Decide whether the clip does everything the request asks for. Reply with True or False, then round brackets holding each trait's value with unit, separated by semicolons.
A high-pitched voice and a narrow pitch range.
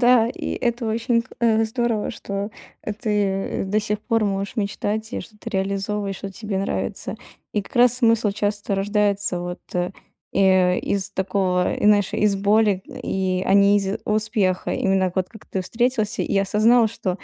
True (205 Hz; 2.1 semitones)